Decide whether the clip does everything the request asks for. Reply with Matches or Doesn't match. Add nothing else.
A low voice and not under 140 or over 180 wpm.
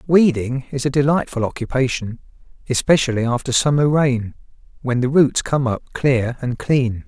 Matches